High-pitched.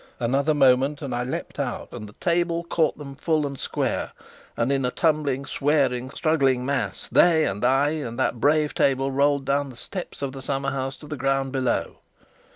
No: medium, 140 Hz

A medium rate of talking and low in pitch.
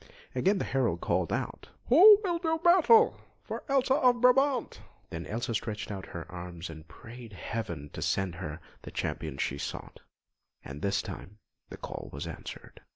Yes: average, 165 wpm; low, 110 Hz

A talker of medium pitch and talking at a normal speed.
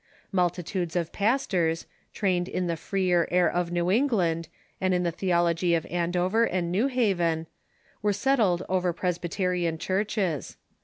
Yes: medium, 180 Hz; average, 145 wpm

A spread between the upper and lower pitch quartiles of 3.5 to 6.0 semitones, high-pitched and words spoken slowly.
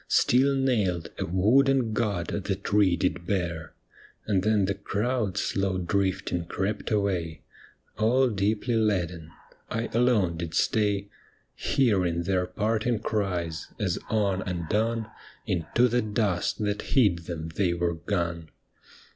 No: average, 4.0 semitones; low, 100 Hz; slow, 130 wpm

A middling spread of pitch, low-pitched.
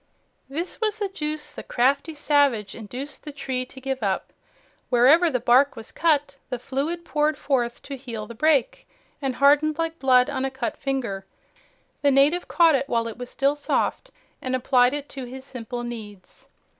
No: average, 3.2 semitones; very high, 270 Hz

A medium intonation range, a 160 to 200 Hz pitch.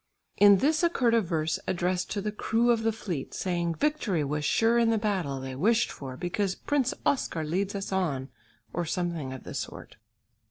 No: wide, 5.8 semitones; high, 190 Hz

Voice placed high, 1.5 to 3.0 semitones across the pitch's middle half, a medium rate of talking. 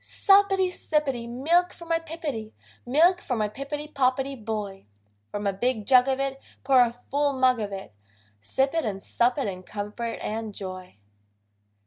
No: very high, 255 Hz; wide, 5.5 semitones; average, 165 wpm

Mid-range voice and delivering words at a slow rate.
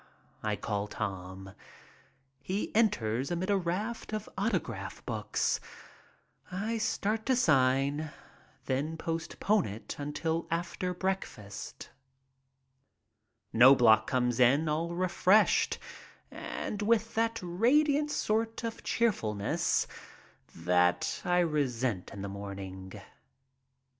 Yes: medium, 155 Hz; slow, 100 wpm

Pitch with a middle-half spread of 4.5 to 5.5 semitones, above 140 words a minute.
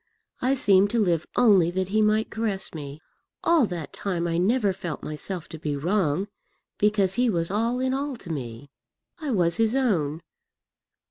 Yes: average, 5.1 semitones; average, 175 wpm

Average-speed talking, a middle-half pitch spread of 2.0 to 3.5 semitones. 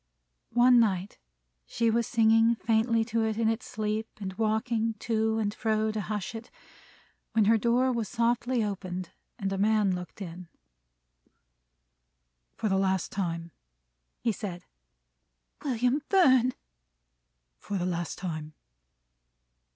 No: slow, 130 wpm; average, 3.1 semitones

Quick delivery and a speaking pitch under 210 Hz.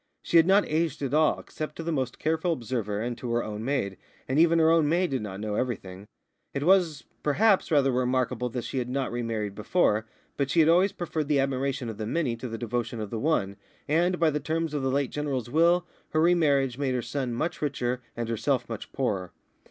Yes: fast, 225 wpm; low, 135 Hz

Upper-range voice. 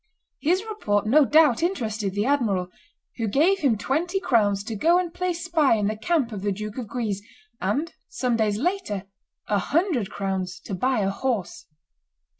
Yes: high, 235 Hz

